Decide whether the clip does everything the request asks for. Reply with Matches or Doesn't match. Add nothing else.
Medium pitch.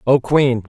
Doesn't match